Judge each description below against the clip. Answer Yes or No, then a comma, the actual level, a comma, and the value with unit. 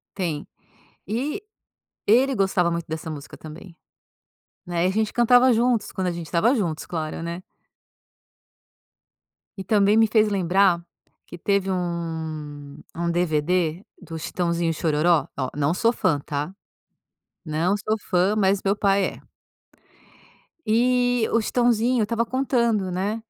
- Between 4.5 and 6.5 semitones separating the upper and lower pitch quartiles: Yes, average, 4.8 semitones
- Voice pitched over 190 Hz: No, medium, 185 Hz